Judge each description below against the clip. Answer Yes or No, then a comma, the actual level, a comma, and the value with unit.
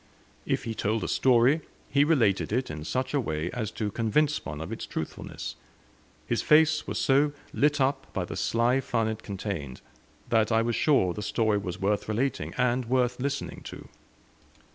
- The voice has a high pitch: No, low, 115 Hz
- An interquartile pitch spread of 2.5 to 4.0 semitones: No, average, 4.5 semitones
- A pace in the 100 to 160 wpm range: No, average, 180 wpm